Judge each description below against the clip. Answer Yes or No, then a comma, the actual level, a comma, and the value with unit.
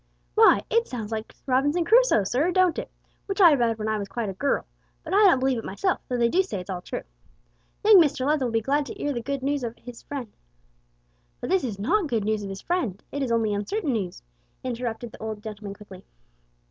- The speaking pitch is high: Yes, high, 245 Hz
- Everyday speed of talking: No, fast, 235 wpm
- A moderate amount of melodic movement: No, wide, 5.8 semitones